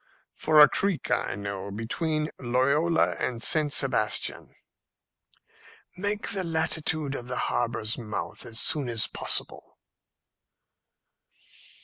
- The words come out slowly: Yes, slow, 105 wpm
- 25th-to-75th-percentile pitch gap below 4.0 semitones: No, wide, 5.6 semitones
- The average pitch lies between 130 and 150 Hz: Yes, medium, 140 Hz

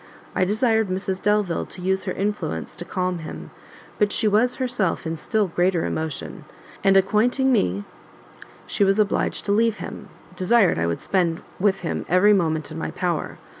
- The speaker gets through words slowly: No, average, 170 wpm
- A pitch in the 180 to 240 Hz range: Yes, high, 190 Hz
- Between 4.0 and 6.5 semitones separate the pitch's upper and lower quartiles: No, average, 3.5 semitones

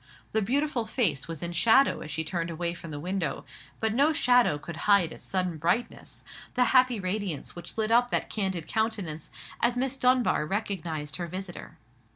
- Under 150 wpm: No, average, 180 wpm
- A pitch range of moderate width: No, wide, 6.1 semitones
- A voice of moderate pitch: No, high, 195 Hz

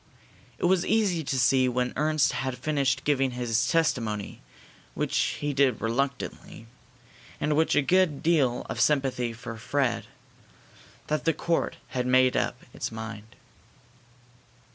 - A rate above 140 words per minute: No, slow, 135 wpm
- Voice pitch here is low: Yes, low, 130 Hz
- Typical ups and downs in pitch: Yes, average, 3.9 semitones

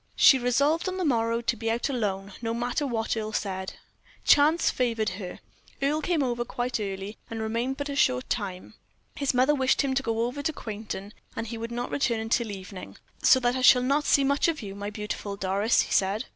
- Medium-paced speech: No, fast, 215 wpm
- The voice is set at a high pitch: Yes, high, 235 Hz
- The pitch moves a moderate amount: Yes, average, 4.2 semitones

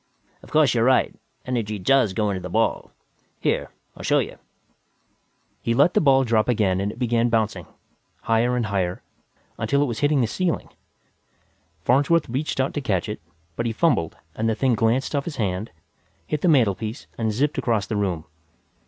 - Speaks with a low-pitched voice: Yes, low, 115 Hz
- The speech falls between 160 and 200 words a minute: Yes, average, 180 wpm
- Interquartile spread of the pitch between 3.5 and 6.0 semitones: Yes, average, 4.1 semitones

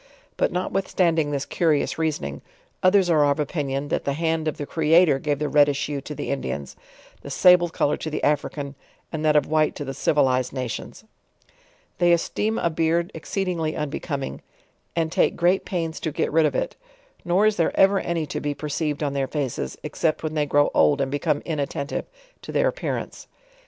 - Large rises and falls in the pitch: No, average, 3.0 semitones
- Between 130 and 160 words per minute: No, average, 190 wpm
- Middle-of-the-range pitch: Yes, medium, 155 Hz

